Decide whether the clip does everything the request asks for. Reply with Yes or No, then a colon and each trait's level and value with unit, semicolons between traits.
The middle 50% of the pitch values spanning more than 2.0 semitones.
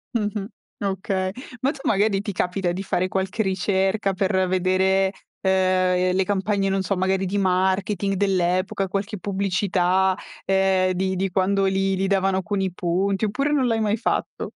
No: narrow, 1.2 semitones